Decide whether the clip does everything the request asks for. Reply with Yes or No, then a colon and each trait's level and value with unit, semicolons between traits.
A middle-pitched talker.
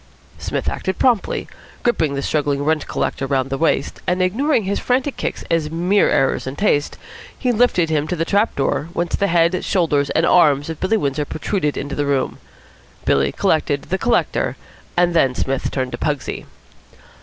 Yes: medium, 160 Hz